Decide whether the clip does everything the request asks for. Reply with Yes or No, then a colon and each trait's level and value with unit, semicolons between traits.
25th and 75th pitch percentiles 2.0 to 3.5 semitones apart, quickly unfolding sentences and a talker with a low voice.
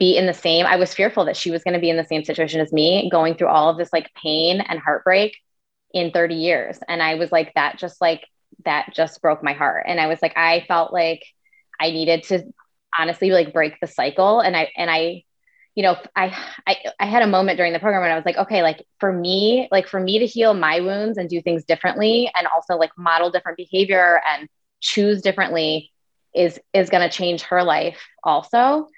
No: average, 2.7 semitones; fast, 225 wpm; medium, 175 Hz